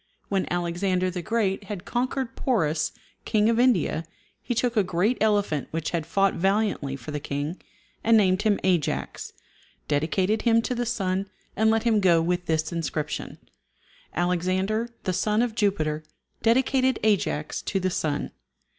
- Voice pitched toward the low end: No, high, 190 Hz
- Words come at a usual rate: Yes, average, 155 wpm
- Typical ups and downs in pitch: Yes, average, 4.6 semitones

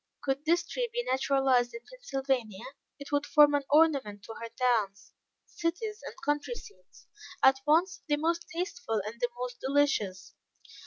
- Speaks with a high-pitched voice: Yes, very high, 280 Hz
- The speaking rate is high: No, average, 155 wpm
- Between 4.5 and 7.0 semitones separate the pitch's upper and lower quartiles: Yes, wide, 5.5 semitones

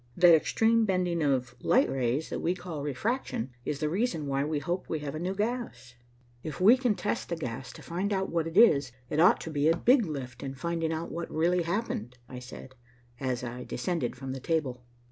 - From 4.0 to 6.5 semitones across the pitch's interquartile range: Yes, average, 5.3 semitones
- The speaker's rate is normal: No, fast, 215 wpm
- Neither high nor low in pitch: Yes, medium, 160 Hz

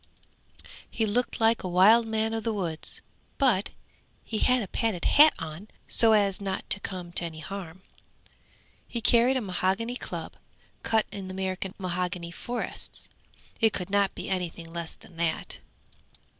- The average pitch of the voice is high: Yes, high, 195 Hz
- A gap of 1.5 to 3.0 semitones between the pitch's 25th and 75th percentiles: No, average, 3.9 semitones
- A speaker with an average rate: Yes, average, 155 wpm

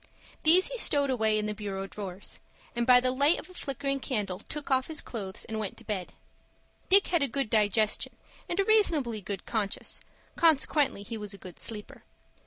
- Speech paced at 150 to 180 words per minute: No, average, 190 wpm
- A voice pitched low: No, high, 235 Hz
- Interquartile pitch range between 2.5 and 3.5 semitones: No, wide, 5.5 semitones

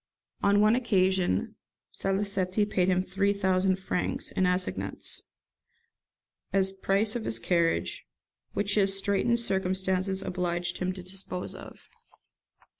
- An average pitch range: No, narrow, 1.5 semitones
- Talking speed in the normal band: No, slow, 120 wpm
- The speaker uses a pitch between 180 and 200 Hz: Yes, high, 190 Hz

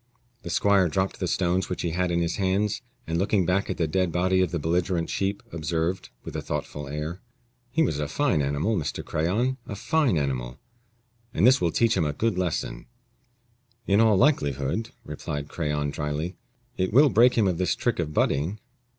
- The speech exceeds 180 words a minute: Yes, average, 190 wpm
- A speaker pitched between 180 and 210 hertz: No, very low, 90 Hz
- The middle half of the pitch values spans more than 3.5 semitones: Yes, average, 4.6 semitones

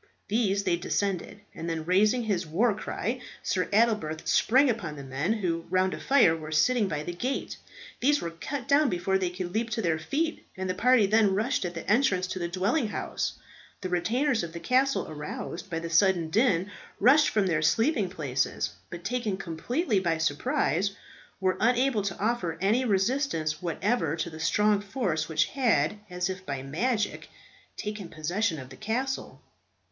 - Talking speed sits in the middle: Yes, average, 180 wpm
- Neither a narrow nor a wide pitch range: No, wide, 5.7 semitones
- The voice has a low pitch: No, high, 190 Hz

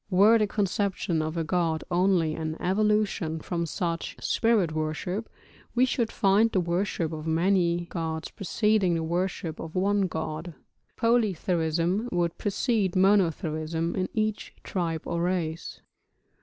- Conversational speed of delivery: No, slow, 130 wpm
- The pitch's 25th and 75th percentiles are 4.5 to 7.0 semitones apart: No, average, 3.7 semitones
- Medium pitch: Yes, medium, 180 Hz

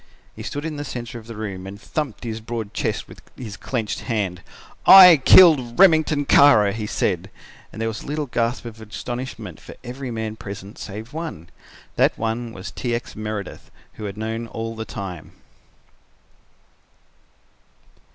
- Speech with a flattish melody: No, average, 3.5 semitones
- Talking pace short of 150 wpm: No, average, 160 wpm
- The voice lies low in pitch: Yes, low, 115 Hz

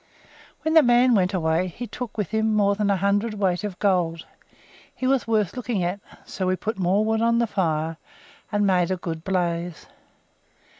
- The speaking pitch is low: No, high, 200 Hz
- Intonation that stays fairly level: No, average, 3.8 semitones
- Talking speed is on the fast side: No, average, 185 wpm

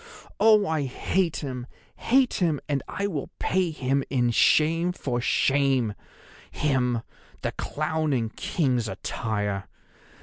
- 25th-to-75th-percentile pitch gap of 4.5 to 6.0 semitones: Yes, average, 5.1 semitones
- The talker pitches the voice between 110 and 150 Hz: Yes, medium, 140 Hz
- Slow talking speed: Yes, slow, 115 wpm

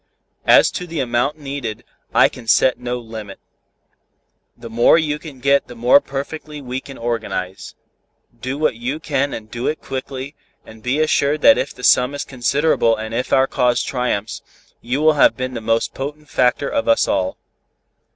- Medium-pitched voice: No, low, 130 Hz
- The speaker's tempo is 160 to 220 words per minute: Yes, average, 175 wpm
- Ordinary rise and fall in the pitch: Yes, average, 3.5 semitones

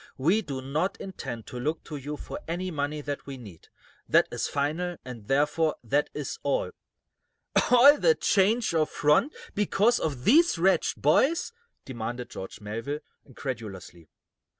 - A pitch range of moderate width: No, wide, 6.2 semitones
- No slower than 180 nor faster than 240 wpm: No, average, 150 wpm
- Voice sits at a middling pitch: Yes, medium, 150 Hz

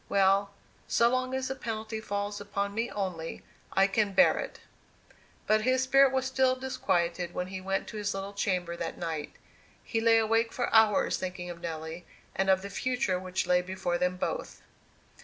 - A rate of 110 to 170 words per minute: No, average, 180 wpm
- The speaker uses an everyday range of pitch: Yes, average, 3.9 semitones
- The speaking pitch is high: Yes, high, 200 Hz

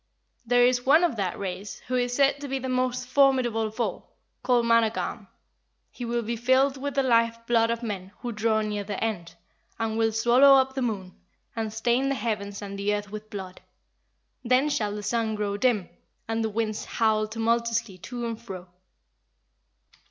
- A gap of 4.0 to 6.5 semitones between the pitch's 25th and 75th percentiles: No, average, 2.9 semitones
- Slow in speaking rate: No, average, 185 wpm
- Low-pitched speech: No, high, 230 Hz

